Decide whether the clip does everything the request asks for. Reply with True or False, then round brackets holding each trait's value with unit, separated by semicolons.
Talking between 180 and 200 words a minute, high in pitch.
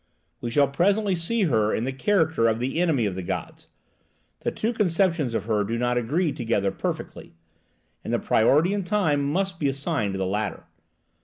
False (185 wpm; 140 Hz)